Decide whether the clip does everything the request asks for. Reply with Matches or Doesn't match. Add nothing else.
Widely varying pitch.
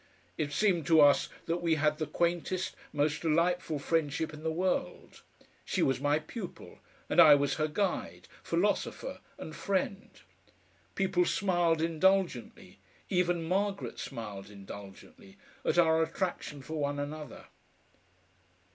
Doesn't match